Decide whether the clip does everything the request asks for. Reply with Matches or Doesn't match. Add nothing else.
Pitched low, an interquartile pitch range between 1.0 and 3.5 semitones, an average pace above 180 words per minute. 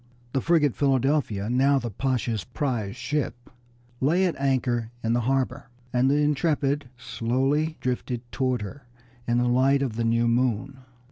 Doesn't match